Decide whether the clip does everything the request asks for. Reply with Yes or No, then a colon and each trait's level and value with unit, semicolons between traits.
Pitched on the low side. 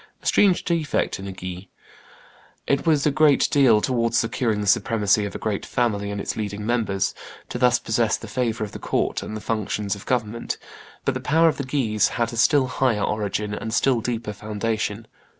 Yes: low, 115 Hz